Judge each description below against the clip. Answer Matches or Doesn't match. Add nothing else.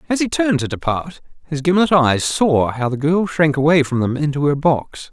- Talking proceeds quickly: Matches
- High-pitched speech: Doesn't match